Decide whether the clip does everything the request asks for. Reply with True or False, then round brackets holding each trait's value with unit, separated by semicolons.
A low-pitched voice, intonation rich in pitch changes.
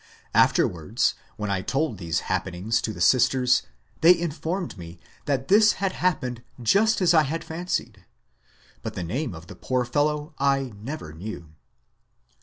True (130 Hz; 7.8 semitones)